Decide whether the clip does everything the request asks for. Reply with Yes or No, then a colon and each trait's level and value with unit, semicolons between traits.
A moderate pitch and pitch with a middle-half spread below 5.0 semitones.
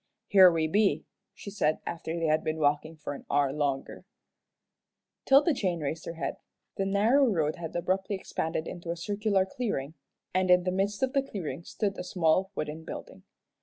Yes: medium, 175 Hz; average, 4.2 semitones